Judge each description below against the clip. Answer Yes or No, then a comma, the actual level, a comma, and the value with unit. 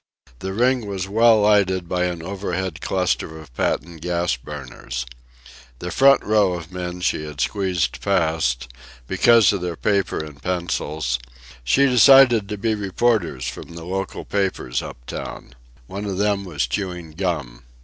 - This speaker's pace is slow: No, average, 155 wpm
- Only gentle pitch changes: No, average, 4.4 semitones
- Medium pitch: No, very low, 90 Hz